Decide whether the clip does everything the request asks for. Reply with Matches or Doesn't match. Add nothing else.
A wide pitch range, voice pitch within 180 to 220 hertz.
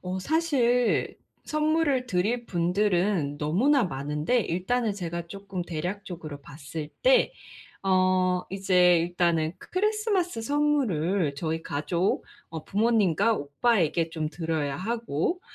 Matches